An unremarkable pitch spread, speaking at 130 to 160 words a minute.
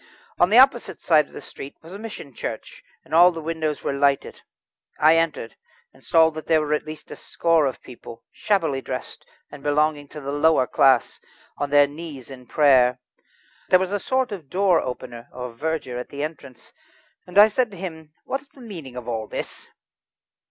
No: average, 4.1 semitones; average, 195 wpm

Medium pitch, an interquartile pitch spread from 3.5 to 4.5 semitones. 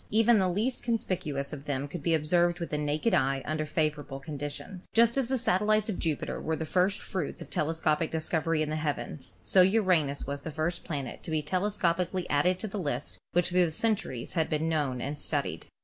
Yes: medium, 160 Hz; average, 4.0 semitones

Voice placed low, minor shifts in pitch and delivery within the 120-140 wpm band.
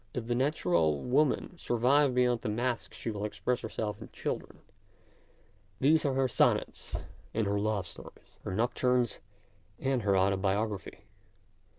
No: low, 120 Hz; average, 3.9 semitones; slow, 135 wpm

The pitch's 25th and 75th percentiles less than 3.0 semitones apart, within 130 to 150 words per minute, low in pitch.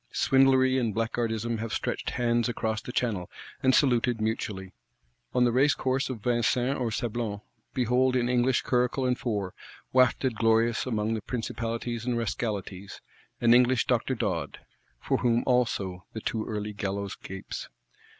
Yes: narrow, 2.4 semitones; average, 140 wpm; low, 115 Hz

